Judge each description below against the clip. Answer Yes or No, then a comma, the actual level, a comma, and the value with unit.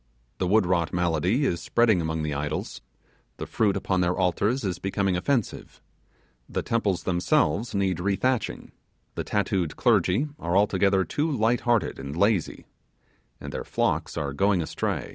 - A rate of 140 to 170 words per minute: Yes, average, 150 wpm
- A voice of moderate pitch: No, very low, 95 Hz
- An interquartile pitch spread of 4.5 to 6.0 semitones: No, average, 3.9 semitones